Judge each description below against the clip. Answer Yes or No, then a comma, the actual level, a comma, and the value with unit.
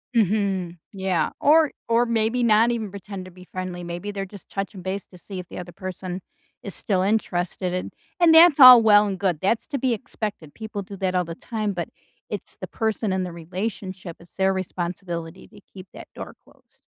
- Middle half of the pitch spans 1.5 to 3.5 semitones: Yes, average, 3.2 semitones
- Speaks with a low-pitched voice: No, high, 195 Hz